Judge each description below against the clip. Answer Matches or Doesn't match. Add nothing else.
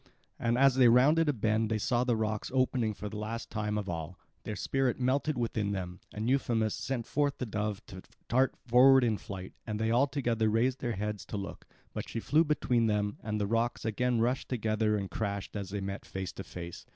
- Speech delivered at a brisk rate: Matches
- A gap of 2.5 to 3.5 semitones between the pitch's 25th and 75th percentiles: Matches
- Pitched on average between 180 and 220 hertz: Doesn't match